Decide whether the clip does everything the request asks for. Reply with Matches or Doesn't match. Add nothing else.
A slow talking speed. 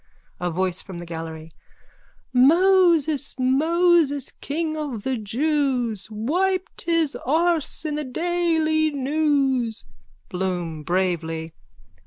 Matches